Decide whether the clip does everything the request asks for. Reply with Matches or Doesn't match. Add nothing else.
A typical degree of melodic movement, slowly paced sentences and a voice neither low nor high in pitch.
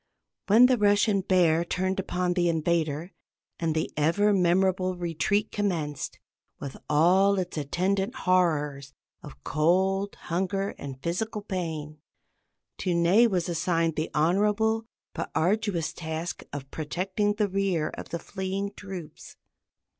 Matches